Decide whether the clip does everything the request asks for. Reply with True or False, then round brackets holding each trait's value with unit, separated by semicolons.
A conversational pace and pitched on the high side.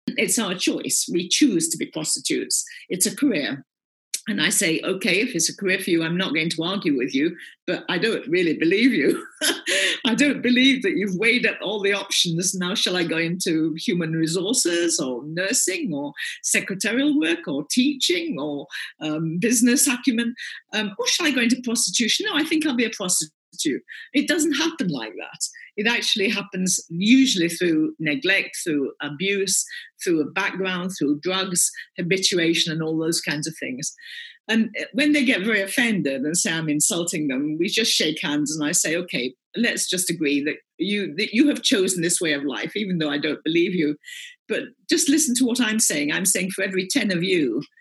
True (195 wpm; 200 Hz)